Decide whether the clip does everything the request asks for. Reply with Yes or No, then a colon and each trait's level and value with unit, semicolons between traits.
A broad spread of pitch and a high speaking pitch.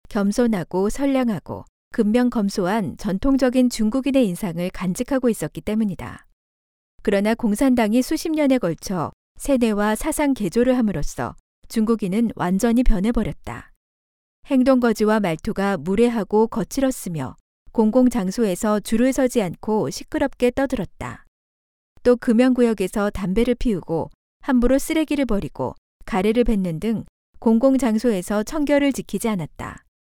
No: average, 4.6 semitones; high, 225 Hz